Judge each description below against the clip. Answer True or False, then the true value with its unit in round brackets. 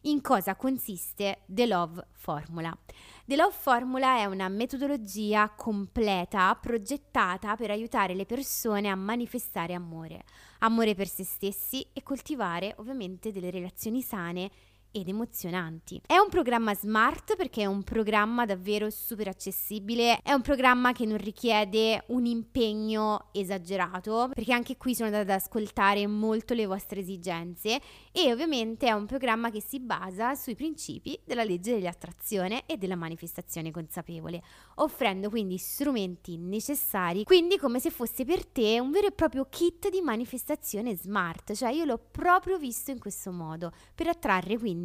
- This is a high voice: True (220 Hz)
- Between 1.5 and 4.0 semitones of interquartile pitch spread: False (4.6 semitones)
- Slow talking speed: False (145 wpm)